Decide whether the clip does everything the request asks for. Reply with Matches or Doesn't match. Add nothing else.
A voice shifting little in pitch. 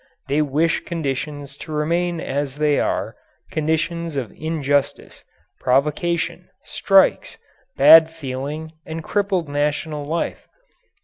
Matches